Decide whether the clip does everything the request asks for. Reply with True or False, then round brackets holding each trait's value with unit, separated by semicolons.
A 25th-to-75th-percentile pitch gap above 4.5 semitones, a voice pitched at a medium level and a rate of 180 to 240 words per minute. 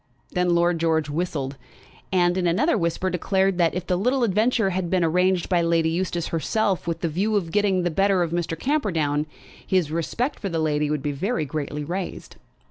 False (2.9 semitones; 175 Hz; 200 wpm)